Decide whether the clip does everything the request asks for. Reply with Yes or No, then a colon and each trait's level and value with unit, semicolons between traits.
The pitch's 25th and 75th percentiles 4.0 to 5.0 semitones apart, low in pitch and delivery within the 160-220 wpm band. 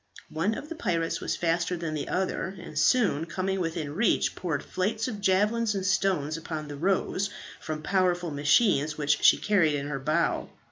No: average, 4.3 semitones; medium, 175 Hz; average, 180 wpm